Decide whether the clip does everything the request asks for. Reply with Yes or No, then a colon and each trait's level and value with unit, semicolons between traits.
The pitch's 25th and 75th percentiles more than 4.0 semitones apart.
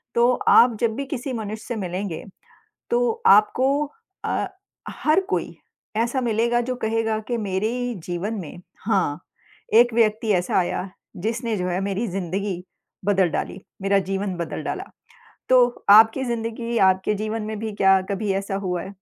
No: average, 3.6 semitones